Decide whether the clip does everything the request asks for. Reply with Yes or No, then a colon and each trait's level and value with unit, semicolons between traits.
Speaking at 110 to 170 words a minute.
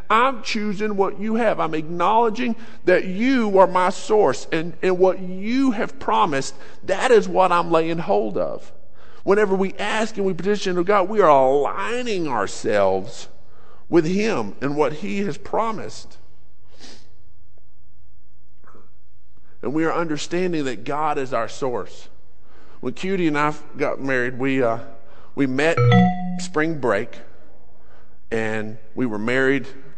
Yes: average, 140 wpm